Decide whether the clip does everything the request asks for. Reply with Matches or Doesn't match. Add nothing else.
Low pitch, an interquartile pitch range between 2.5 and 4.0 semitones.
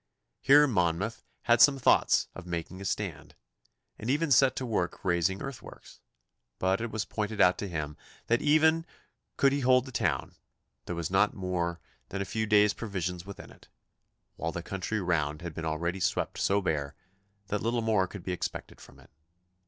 Doesn't match